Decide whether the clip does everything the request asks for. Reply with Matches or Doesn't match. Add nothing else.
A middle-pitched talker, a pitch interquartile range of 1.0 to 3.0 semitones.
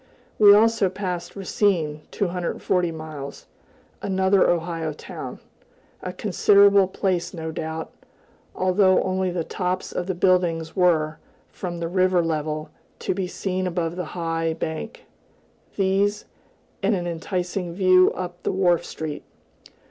Matches